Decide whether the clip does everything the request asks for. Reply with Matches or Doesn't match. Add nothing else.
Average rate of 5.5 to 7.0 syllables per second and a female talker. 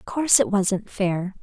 Doesn't match